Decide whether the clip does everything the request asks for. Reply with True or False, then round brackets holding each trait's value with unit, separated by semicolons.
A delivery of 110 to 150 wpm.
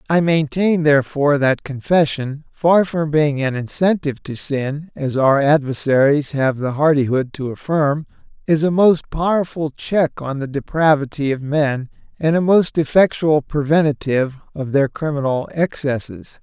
True (140 wpm)